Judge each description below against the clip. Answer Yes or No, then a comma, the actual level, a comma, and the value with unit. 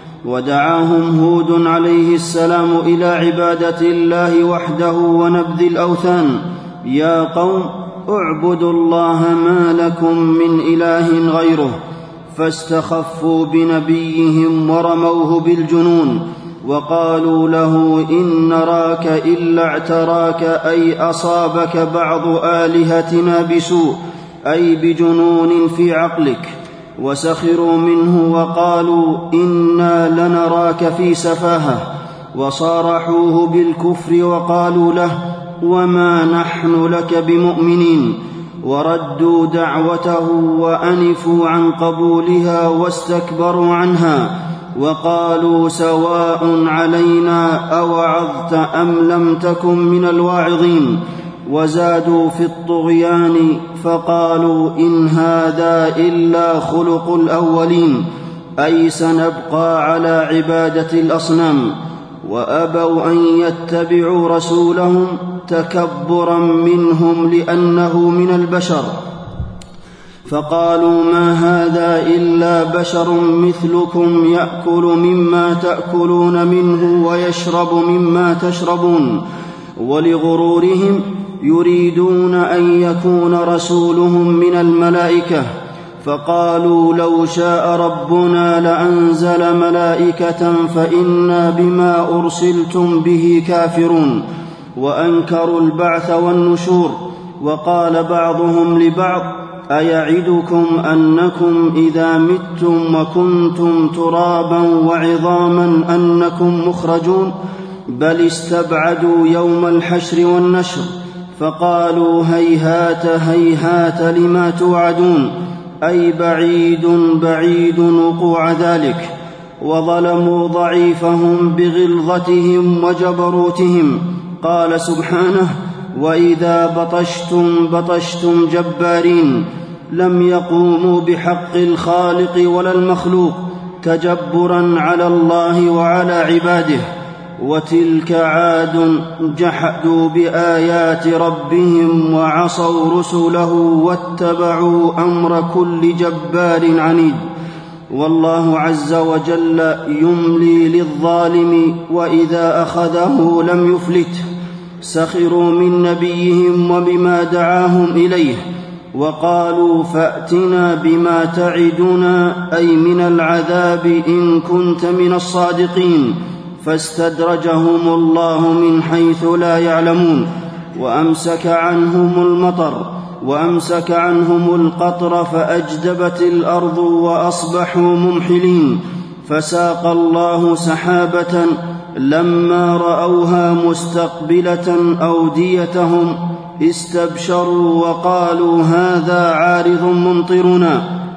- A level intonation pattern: Yes, narrow, 0.8 semitones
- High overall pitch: No, medium, 170 Hz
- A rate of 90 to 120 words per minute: No, average, 75 wpm